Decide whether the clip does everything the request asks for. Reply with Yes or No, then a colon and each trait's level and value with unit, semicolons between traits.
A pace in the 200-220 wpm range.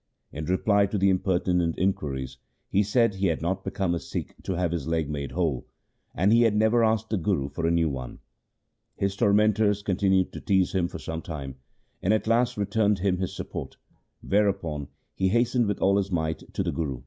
Yes: fast, 205 wpm